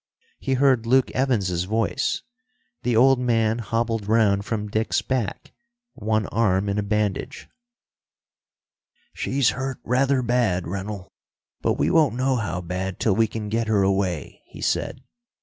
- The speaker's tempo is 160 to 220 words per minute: No, average, 145 wpm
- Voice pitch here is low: Yes, low, 110 Hz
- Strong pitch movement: No, average, 3.9 semitones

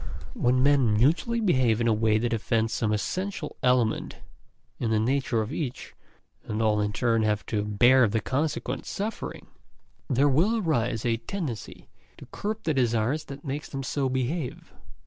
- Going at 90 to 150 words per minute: No, average, 165 wpm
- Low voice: Yes, low, 125 Hz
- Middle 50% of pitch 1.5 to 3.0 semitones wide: No, average, 4.4 semitones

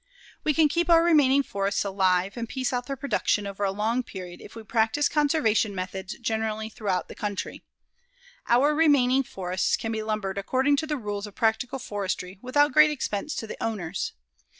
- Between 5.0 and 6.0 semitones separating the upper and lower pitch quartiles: Yes, wide, 5.5 semitones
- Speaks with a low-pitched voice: No, high, 225 Hz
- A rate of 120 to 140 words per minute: No, average, 180 wpm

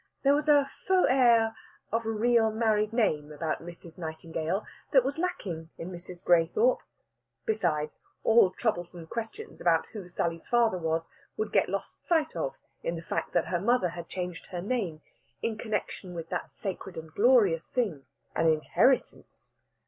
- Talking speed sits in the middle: Yes, average, 160 wpm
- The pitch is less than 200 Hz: Yes, high, 190 Hz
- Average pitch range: No, wide, 6.1 semitones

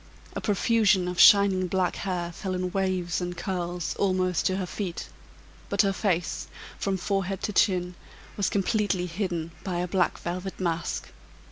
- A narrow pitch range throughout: Yes, narrow, 1.8 semitones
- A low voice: No, medium, 185 Hz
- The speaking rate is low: No, average, 155 wpm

